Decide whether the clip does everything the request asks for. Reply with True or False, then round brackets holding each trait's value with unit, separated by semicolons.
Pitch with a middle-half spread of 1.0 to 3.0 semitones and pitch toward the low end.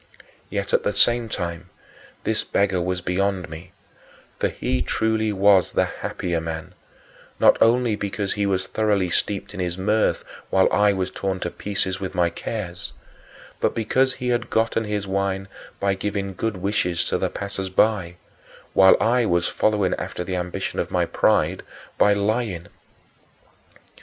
True (2.6 semitones; 100 Hz)